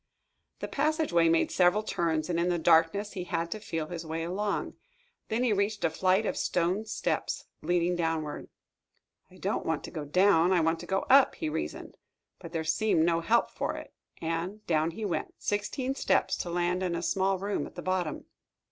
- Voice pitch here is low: No, medium, 175 Hz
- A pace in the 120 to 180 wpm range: No, average, 195 wpm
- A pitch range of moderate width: Yes, average, 3.5 semitones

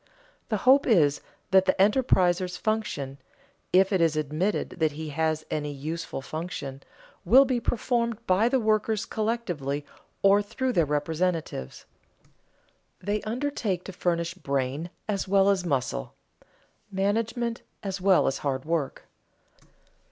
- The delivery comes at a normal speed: No, slow, 130 wpm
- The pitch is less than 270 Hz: Yes, medium, 185 Hz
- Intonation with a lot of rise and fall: Yes, wide, 5.8 semitones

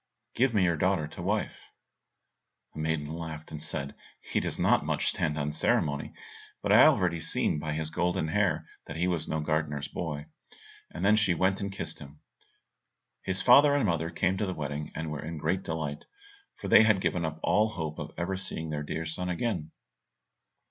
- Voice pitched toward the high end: No, very low, 80 Hz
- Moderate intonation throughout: Yes, average, 3.3 semitones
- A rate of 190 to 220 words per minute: Yes, average, 195 wpm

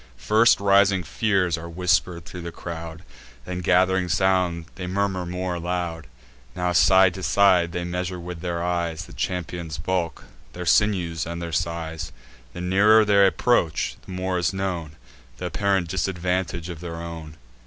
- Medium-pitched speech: No, very low, 90 Hz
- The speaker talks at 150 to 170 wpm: Yes, average, 155 wpm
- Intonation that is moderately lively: No, narrow, 1.9 semitones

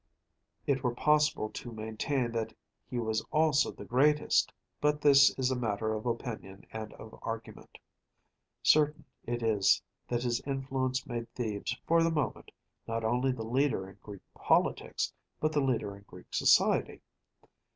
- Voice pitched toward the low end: Yes, low, 120 Hz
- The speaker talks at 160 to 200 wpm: No, average, 150 wpm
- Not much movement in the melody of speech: No, average, 4.0 semitones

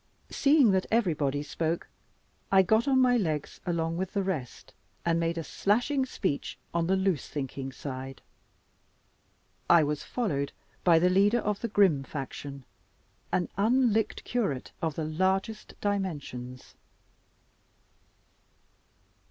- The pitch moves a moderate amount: No, wide, 5.9 semitones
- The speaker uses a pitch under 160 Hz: No, medium, 175 Hz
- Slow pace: Yes, slow, 125 wpm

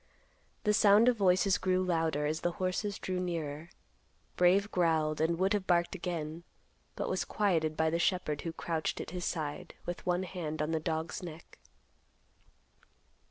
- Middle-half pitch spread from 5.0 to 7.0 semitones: No, average, 2.7 semitones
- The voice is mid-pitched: Yes, medium, 175 Hz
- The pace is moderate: Yes, average, 160 wpm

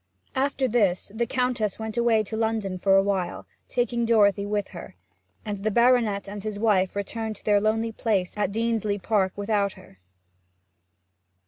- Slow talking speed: No, average, 160 wpm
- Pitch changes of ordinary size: No, narrow, 2.3 semitones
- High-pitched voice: Yes, high, 215 Hz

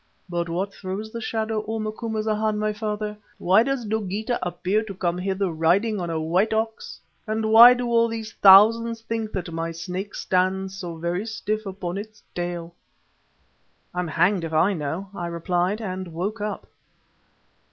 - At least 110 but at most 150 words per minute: No, average, 165 wpm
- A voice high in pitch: Yes, high, 200 Hz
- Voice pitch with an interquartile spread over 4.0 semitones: No, average, 3.6 semitones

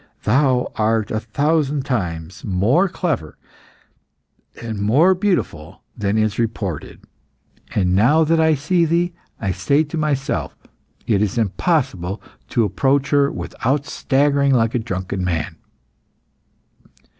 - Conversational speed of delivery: No, slow, 120 wpm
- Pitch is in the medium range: No, low, 120 Hz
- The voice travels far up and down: Yes, wide, 6.8 semitones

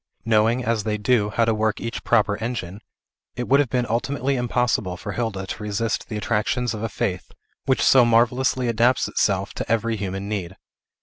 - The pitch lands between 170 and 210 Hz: No, low, 115 Hz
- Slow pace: No, average, 185 wpm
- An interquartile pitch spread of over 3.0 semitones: No, average, 2.7 semitones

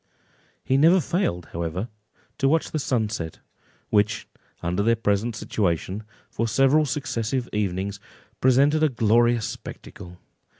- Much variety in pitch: No, average, 5.0 semitones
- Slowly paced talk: Yes, slow, 120 wpm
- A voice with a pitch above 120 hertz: No, low, 115 Hz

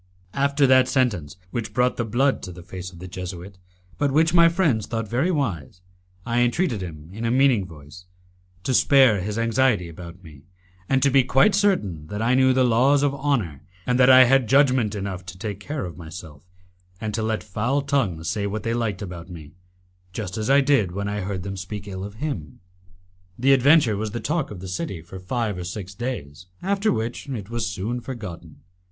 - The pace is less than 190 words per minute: No, fast, 205 wpm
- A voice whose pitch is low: Yes, low, 110 Hz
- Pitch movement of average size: No, wide, 6.2 semitones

